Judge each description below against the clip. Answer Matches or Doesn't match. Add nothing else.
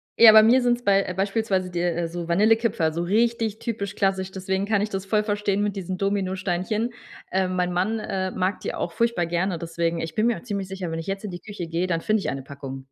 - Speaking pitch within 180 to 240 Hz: Matches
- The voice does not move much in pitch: Doesn't match